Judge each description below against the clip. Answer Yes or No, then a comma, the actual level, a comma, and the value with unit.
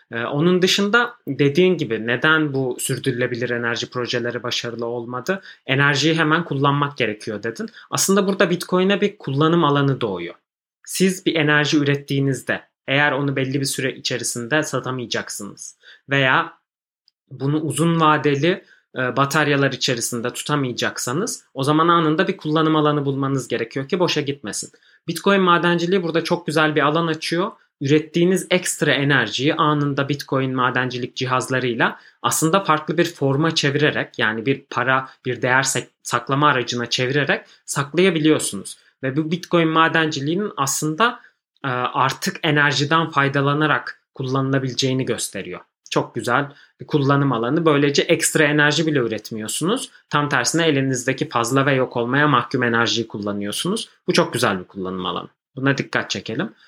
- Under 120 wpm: No, average, 125 wpm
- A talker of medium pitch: Yes, medium, 145 Hz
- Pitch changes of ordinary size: Yes, average, 4.1 semitones